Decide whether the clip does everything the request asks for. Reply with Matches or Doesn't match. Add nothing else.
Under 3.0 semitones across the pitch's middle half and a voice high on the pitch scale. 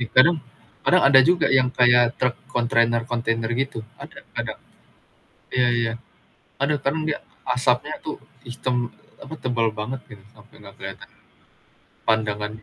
Doesn't match